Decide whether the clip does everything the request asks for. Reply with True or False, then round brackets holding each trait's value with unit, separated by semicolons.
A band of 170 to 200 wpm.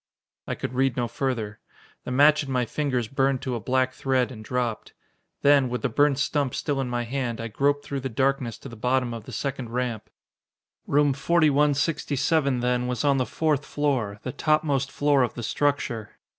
True (190 wpm)